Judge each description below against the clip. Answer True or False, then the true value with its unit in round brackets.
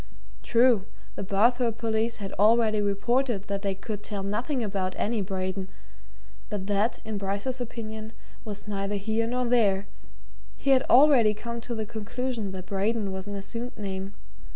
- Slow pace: False (155 wpm)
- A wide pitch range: False (3.0 semitones)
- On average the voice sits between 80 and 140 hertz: False (215 Hz)